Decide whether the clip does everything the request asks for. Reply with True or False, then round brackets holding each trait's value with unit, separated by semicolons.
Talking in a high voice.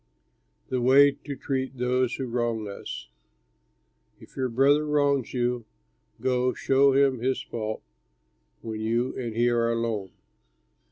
False (125 Hz)